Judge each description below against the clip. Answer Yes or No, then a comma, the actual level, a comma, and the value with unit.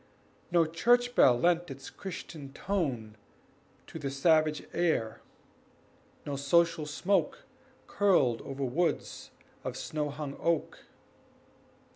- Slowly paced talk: Yes, slow, 105 wpm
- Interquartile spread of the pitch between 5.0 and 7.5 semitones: No, average, 4.1 semitones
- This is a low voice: No, medium, 155 Hz